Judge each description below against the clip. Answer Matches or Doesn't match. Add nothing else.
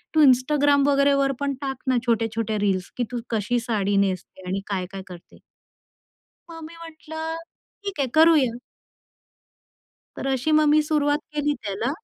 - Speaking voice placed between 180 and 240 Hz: Doesn't match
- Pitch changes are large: Matches